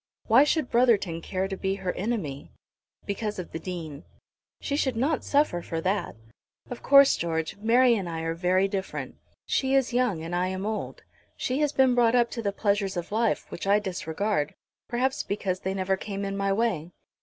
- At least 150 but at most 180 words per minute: No, average, 190 wpm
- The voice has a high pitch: Yes, high, 200 Hz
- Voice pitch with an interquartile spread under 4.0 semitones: No, average, 4.7 semitones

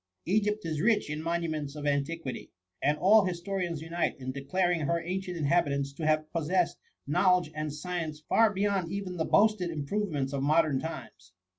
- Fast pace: No, average, 165 wpm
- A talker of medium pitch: Yes, medium, 165 Hz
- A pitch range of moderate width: Yes, average, 3.6 semitones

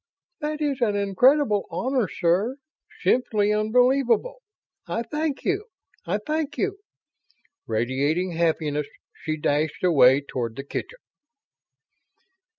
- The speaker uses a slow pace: Yes, slow, 105 wpm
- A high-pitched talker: Yes, high, 210 Hz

